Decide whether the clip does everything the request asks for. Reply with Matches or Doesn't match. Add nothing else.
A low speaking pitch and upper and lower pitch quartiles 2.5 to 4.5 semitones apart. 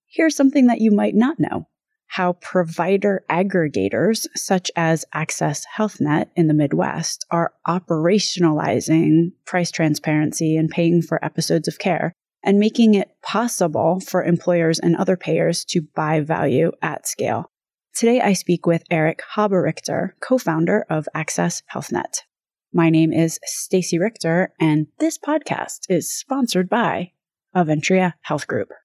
Doesn't match